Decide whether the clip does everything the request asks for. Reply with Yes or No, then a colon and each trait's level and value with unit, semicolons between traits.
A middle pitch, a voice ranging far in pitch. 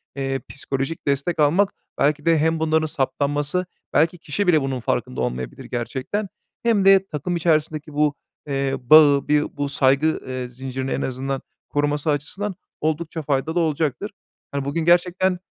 No: medium, 150 Hz; average, 3.2 semitones